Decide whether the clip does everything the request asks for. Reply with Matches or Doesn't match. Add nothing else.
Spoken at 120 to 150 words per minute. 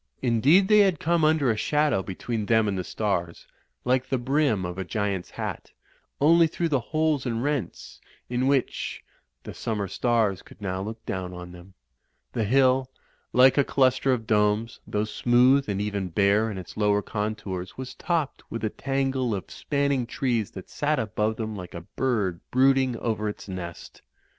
Doesn't match